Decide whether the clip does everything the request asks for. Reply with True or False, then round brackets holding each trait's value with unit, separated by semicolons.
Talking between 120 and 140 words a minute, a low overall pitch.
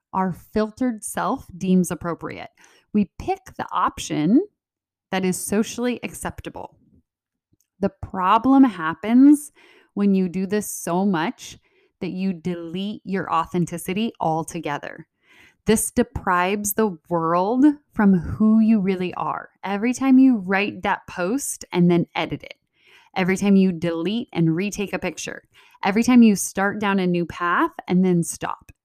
False (135 wpm; 195 Hz)